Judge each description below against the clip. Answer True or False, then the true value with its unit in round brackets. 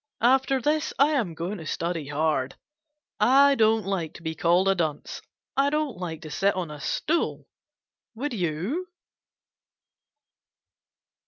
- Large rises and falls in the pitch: True (8.9 semitones)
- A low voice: False (195 Hz)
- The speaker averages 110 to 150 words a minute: True (140 wpm)